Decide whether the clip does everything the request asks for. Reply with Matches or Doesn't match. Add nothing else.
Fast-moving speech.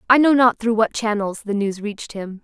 Matches